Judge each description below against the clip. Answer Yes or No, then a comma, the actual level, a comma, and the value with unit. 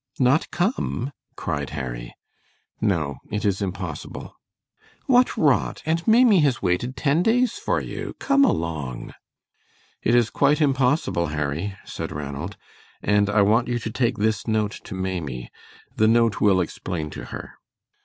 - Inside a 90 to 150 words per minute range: Yes, average, 145 wpm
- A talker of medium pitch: No, low, 105 Hz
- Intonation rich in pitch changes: Yes, wide, 7.9 semitones